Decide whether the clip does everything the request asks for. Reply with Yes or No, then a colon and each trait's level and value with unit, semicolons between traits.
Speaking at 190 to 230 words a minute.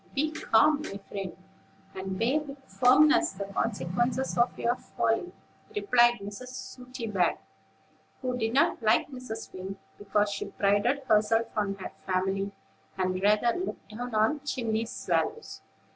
No: slow, 135 wpm